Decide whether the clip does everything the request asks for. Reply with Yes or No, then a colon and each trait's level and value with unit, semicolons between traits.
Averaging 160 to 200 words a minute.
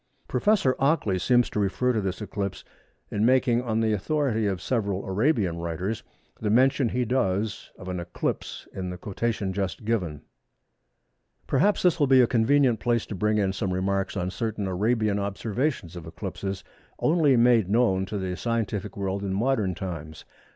Yes: average, 165 wpm